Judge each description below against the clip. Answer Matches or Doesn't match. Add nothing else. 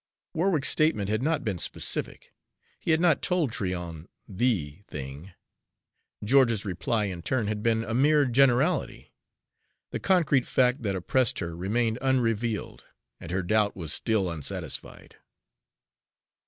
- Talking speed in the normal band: Doesn't match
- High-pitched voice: Doesn't match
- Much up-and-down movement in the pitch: Matches